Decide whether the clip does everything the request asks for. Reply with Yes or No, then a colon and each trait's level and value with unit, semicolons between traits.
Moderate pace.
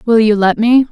No: fast, 260 wpm